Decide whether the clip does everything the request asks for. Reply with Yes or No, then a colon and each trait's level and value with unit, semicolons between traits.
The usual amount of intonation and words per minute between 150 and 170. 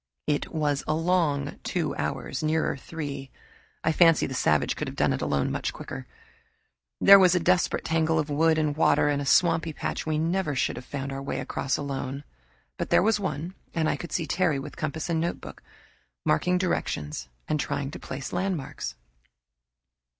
No: average, 3.1 semitones; average, 180 wpm